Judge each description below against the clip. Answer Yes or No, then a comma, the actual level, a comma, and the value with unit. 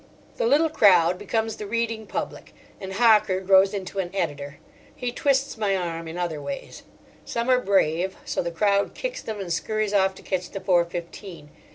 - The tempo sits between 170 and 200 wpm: Yes, average, 185 wpm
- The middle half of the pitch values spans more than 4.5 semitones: No, average, 4.0 semitones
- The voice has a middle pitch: No, high, 195 Hz